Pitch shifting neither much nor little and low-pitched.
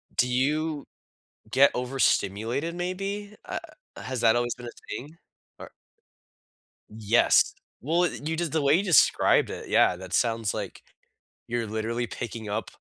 No: wide, 5.9 semitones; low, 125 Hz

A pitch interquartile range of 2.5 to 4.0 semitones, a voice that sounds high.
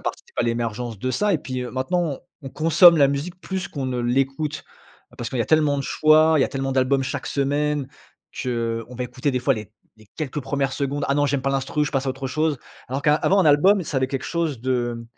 No: average, 2.9 semitones; low, 135 Hz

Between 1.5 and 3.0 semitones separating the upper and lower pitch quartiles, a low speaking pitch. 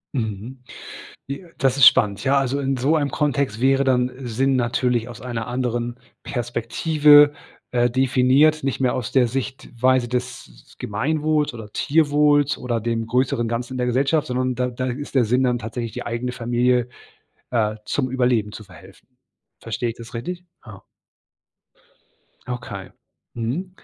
Yes: narrow, 2.5 semitones; low, 125 Hz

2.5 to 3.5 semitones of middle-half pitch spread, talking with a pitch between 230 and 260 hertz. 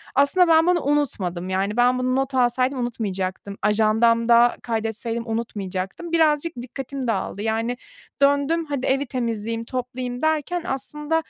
No: average, 4.1 semitones; high, 245 Hz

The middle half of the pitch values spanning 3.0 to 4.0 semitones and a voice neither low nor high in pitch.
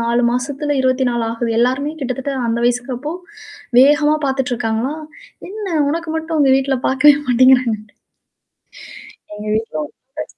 No: average, 3.3 semitones; very high, 260 Hz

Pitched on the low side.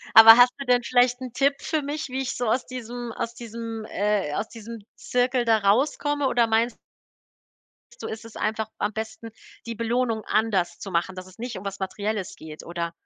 No: high, 230 Hz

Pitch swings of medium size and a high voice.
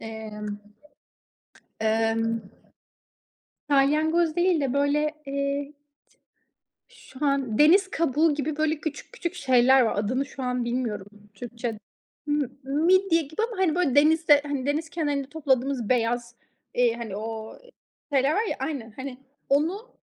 Yes: average, 4.3 semitones; very high, 280 Hz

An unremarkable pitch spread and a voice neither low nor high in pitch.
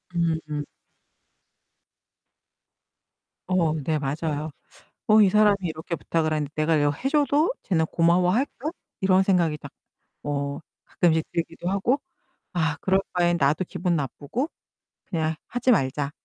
Yes: average, 3.8 semitones; medium, 165 Hz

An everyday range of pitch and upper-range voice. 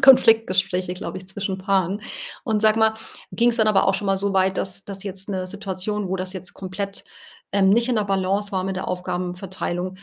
No: narrow, 1.8 semitones; high, 195 Hz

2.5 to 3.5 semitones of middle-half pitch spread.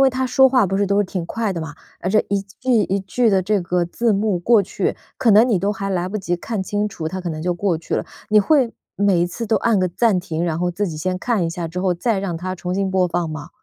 Yes: average, 3.2 semitones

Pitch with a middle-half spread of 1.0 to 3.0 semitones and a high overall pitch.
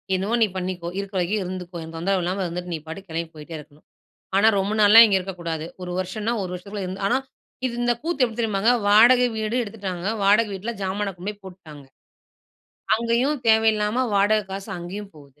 No: average, 3.5 semitones; high, 195 Hz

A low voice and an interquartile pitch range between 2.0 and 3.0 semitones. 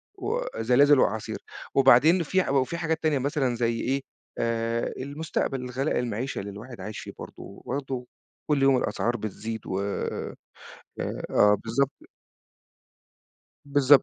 No: low, 130 Hz; average, 3.7 semitones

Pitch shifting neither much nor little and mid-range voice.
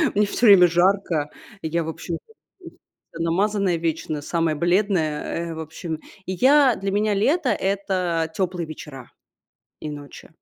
Yes: average, 3.7 semitones; medium, 175 Hz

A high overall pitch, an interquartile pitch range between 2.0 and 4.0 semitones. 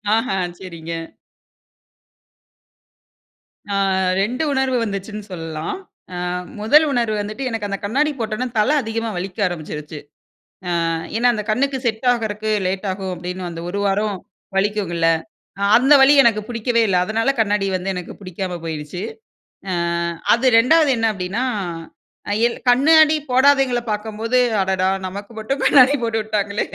No: high, 215 Hz; average, 4.4 semitones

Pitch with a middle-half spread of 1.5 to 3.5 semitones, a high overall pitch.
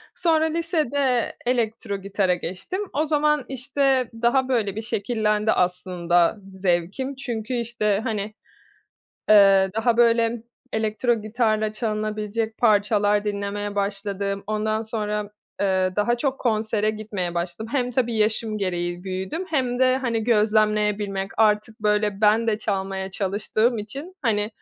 Yes: average, 2.9 semitones; high, 215 Hz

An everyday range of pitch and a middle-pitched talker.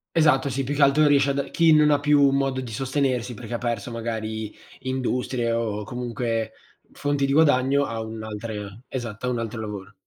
No: average, 3.7 semitones; low, 125 Hz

